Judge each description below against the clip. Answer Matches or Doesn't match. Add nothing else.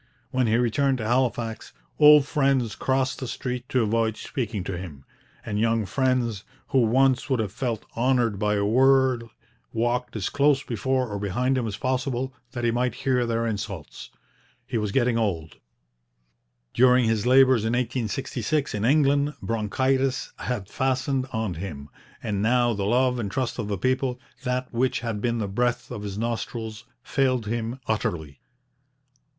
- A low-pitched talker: Matches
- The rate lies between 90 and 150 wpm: Doesn't match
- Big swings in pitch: Doesn't match